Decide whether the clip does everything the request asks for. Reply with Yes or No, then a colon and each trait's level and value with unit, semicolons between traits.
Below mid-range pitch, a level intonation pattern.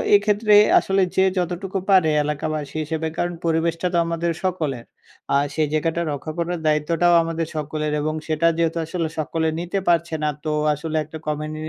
No: medium, 165 Hz; narrow, 2.1 semitones